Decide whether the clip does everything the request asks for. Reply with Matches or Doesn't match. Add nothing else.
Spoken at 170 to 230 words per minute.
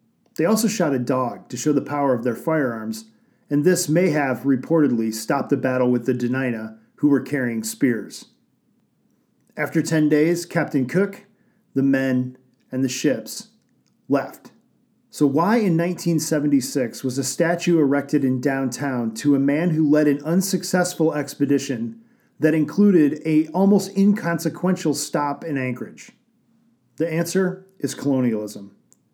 Doesn't match